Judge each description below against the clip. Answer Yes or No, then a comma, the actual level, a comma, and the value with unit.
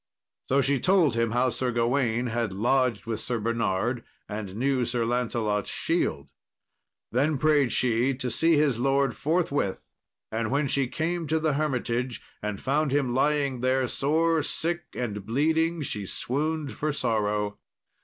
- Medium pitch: No, low, 130 Hz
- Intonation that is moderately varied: Yes, average, 4.2 semitones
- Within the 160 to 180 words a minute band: No, average, 150 wpm